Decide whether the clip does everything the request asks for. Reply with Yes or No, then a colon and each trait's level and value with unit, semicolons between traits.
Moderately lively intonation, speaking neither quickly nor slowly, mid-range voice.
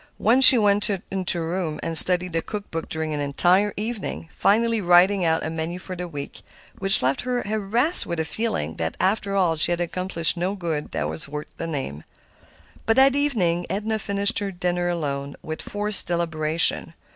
Yes: average, 4.1 semitones; average, 185 wpm; medium, 180 Hz